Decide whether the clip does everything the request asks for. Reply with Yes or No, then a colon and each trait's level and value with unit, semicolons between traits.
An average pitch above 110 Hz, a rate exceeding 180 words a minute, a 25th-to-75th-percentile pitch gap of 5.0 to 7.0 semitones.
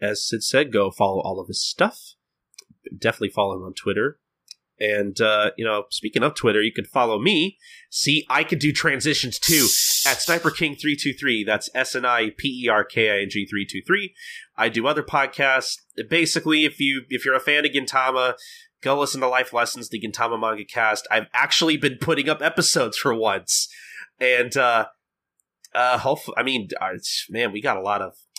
Yes: low, 135 Hz; average, 200 wpm; wide, 5.5 semitones